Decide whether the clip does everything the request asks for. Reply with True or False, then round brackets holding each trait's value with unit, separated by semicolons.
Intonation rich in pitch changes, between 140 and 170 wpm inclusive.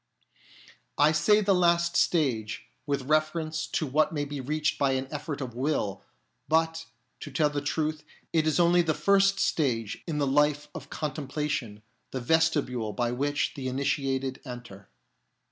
False (3.2 semitones; 160 wpm)